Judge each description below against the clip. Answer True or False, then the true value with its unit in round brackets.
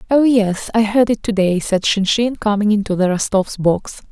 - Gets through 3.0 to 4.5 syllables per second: False (4.8 syllables/s)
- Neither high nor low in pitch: False (210 Hz)